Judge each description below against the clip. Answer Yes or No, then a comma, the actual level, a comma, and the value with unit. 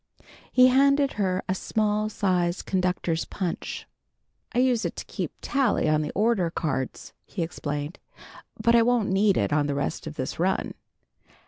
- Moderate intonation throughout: No, wide, 6.1 semitones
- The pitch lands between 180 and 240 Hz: Yes, high, 190 Hz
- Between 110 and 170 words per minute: Yes, average, 160 wpm